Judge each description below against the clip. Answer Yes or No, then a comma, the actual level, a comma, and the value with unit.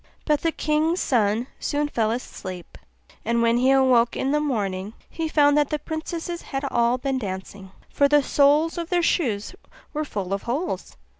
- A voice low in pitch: No, very high, 270 Hz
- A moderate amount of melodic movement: Yes, average, 5.0 semitones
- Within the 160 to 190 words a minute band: Yes, average, 175 wpm